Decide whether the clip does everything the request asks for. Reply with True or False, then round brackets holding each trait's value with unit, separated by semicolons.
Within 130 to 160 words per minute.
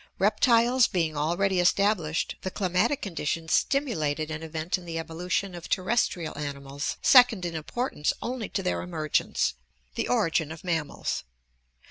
True (140 wpm)